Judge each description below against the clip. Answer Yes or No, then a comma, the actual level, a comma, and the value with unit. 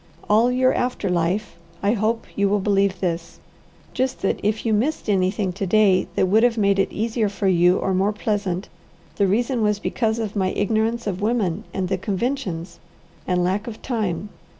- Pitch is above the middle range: Yes, high, 205 Hz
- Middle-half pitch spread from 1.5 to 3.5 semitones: Yes, average, 3.0 semitones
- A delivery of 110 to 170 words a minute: No, average, 185 wpm